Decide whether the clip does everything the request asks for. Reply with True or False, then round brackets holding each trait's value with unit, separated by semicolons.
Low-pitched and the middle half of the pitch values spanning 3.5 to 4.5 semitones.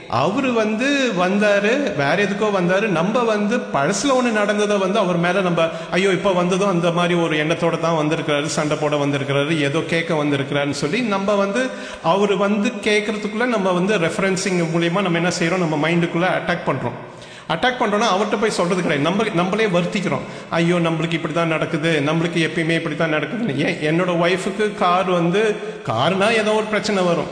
False (180 Hz; 4.2 semitones)